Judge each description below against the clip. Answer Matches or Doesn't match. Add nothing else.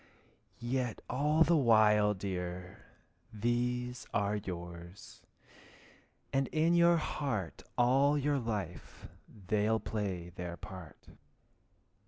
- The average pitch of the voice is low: Matches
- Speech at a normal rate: Doesn't match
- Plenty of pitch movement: Matches